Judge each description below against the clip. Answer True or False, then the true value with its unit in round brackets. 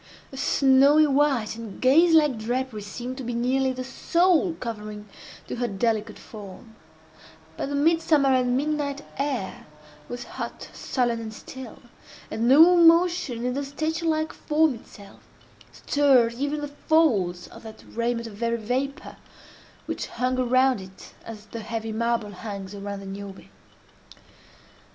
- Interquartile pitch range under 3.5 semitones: False (4.6 semitones)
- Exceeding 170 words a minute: False (145 wpm)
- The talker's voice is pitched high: True (250 Hz)